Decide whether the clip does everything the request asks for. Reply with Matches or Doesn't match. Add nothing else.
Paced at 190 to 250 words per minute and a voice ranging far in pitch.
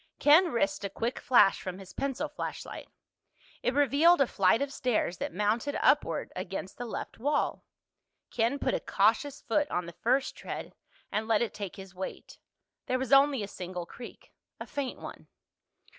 Doesn't match